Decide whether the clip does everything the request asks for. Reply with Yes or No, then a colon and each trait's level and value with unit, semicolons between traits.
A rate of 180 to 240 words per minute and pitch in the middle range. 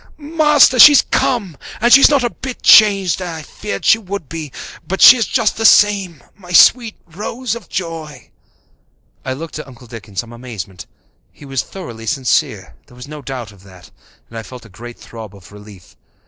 Yes: average, 190 wpm; medium, 160 Hz